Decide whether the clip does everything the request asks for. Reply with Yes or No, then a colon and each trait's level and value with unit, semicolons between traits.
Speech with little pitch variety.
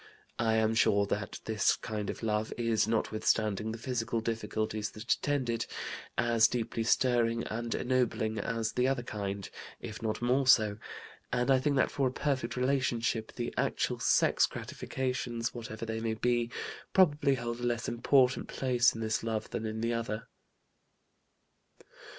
Yes: narrow, 2.0 semitones